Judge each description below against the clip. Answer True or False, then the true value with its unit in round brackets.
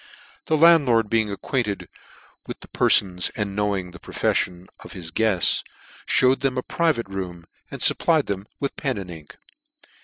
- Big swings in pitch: True (6.0 semitones)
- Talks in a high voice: False (105 Hz)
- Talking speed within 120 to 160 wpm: True (155 wpm)